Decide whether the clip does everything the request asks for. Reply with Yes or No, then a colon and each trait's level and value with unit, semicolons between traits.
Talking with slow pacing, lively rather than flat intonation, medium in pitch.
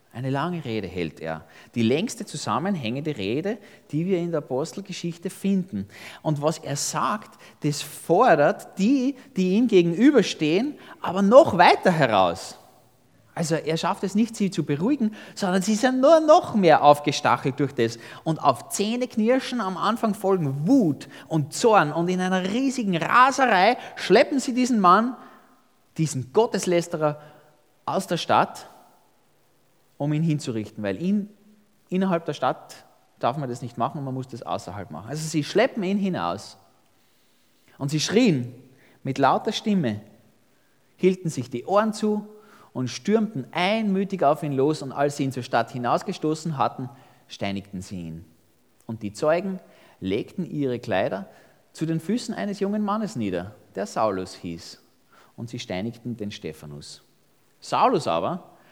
No: average, 145 wpm; wide, 8.4 semitones; medium, 155 Hz